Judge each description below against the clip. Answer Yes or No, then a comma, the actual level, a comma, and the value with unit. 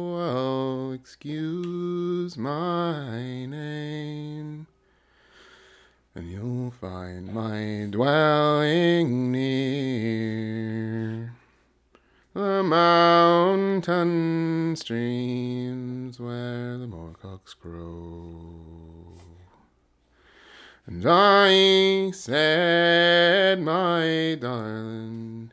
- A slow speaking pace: Yes, slow, 50 wpm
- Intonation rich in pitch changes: Yes, wide, 7.2 semitones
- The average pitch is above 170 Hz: No, low, 130 Hz